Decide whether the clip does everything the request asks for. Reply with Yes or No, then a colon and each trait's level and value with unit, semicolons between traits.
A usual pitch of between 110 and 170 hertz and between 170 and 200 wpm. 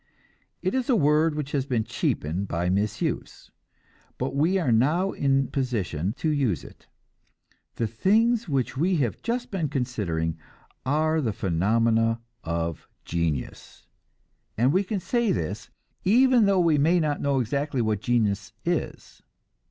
No: low, 135 Hz; average, 145 wpm